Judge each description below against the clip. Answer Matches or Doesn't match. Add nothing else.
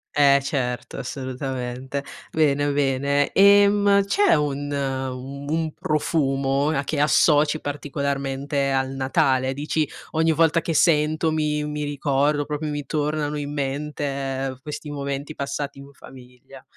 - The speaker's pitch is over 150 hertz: Doesn't match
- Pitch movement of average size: Doesn't match